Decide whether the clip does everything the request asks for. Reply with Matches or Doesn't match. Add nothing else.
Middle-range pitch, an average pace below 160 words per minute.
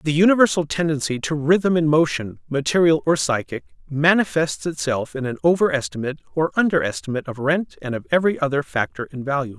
Doesn't match